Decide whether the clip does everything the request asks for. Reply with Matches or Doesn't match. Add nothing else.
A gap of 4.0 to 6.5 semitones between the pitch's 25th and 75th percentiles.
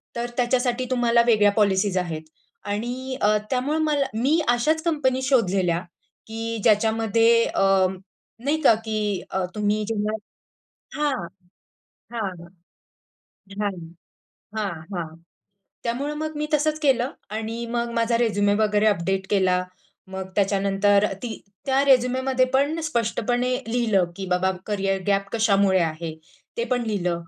Matches